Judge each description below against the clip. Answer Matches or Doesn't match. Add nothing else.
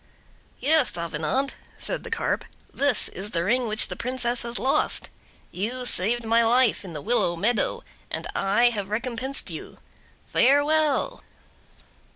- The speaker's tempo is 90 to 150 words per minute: Matches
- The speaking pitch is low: Doesn't match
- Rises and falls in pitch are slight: Doesn't match